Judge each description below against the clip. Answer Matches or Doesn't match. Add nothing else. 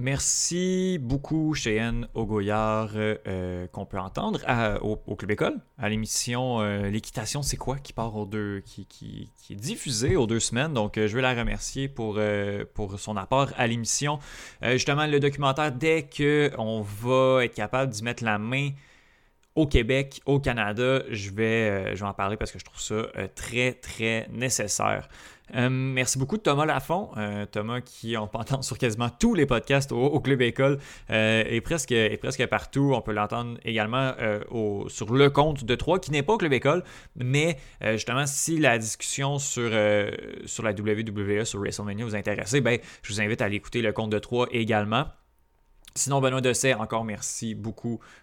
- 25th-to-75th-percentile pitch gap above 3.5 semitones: Matches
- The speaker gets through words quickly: Doesn't match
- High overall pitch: Doesn't match